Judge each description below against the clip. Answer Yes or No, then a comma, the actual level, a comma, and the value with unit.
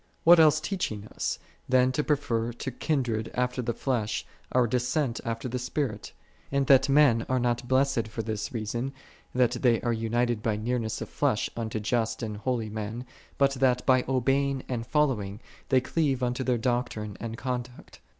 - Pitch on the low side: Yes, low, 125 Hz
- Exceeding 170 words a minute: Yes, average, 180 wpm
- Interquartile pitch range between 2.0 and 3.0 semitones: Yes, average, 2.7 semitones